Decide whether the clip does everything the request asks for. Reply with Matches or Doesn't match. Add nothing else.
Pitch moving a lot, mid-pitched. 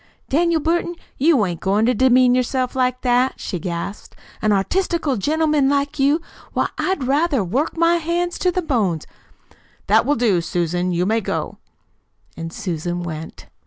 Doesn't match